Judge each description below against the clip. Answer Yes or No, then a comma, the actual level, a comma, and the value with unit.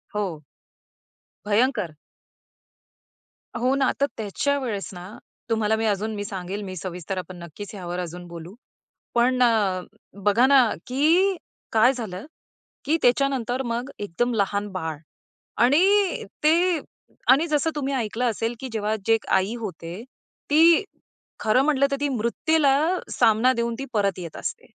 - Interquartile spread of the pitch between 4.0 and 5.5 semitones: Yes, average, 5.1 semitones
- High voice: Yes, high, 225 Hz